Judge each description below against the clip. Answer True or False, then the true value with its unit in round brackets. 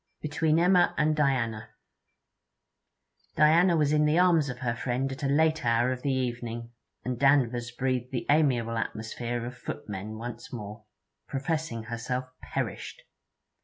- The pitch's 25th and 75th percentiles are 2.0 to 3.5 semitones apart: False (4.2 semitones)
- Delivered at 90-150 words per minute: True (140 wpm)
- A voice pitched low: True (125 Hz)